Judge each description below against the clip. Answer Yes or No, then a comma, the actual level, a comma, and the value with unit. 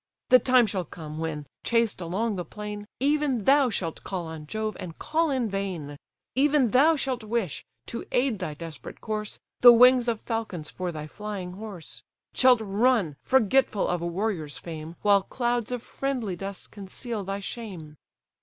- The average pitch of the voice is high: Yes, high, 210 Hz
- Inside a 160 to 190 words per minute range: Yes, average, 165 wpm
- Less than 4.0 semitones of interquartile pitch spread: No, wide, 5.5 semitones